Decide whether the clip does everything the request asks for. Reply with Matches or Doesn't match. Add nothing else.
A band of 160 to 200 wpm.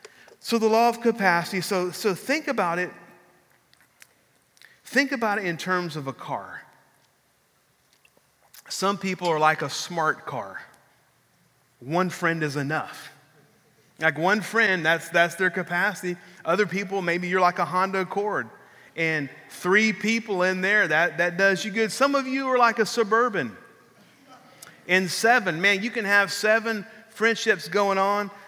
Doesn't match